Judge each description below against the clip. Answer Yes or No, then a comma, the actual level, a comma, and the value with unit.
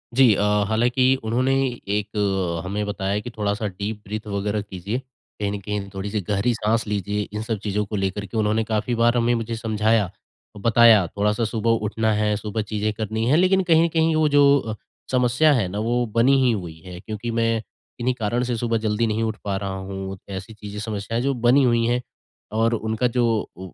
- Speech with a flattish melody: Yes, narrow, 2.3 semitones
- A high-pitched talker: No, low, 110 Hz